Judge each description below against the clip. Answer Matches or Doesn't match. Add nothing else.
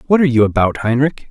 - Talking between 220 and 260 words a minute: Matches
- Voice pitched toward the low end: Matches